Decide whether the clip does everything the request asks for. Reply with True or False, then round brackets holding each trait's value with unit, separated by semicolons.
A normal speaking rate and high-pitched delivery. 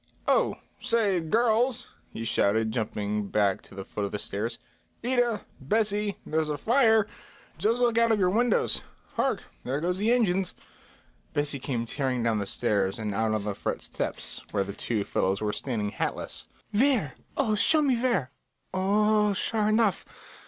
False (170 wpm; 180 Hz)